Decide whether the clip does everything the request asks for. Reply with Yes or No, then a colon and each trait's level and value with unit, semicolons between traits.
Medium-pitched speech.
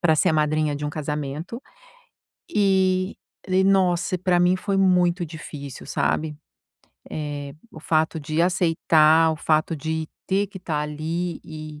Yes: medium, 160 Hz